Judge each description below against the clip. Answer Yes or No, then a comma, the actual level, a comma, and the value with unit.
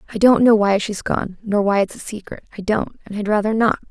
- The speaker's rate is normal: No, fast, 245 wpm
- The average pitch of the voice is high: Yes, high, 210 Hz